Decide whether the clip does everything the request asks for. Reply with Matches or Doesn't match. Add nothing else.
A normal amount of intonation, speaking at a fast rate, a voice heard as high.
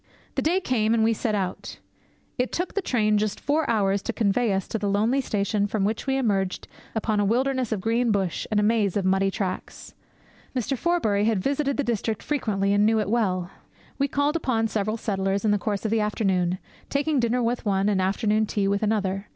Matches